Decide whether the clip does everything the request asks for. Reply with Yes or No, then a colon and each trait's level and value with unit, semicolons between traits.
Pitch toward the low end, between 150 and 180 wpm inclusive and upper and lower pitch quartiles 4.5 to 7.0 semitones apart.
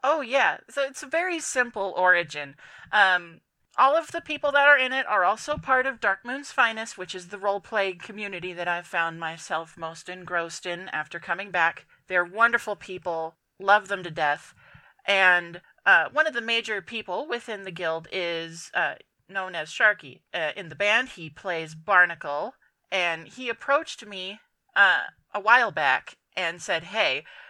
No: high, 190 Hz; average, 170 wpm; wide, 5.4 semitones